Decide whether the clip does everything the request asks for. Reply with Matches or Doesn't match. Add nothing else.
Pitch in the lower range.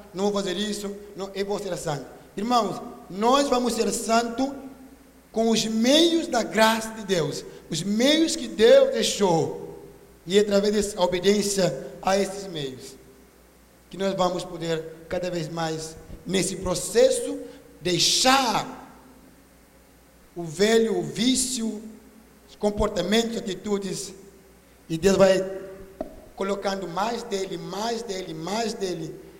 Doesn't match